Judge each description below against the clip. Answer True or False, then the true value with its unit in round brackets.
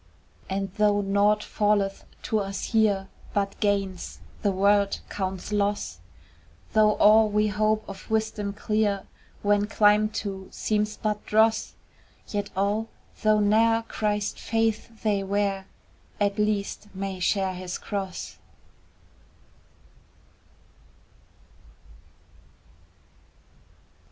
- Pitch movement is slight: True (1.4 semitones)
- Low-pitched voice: False (205 Hz)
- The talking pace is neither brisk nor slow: False (100 wpm)